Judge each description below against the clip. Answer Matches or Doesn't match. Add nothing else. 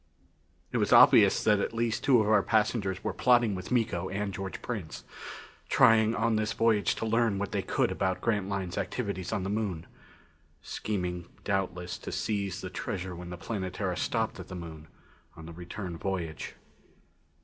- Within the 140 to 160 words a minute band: Doesn't match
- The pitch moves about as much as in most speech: Matches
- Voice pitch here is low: Matches